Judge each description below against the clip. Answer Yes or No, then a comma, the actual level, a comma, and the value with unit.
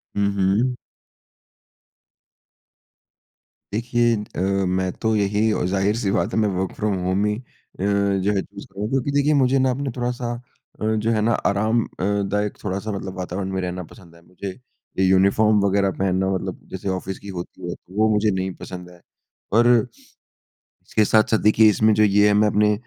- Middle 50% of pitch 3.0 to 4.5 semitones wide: No, narrow, 2.4 semitones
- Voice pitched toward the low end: Yes, low, 105 Hz